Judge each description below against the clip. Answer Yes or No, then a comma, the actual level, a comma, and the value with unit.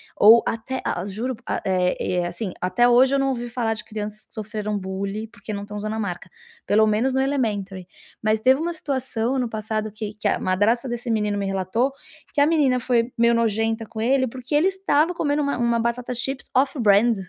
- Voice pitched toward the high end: Yes, high, 225 Hz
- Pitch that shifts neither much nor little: Yes, average, 3.6 semitones